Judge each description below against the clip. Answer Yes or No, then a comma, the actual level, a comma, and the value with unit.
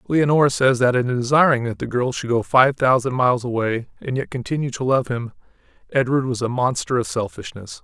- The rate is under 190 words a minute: No, average, 200 wpm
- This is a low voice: Yes, low, 125 Hz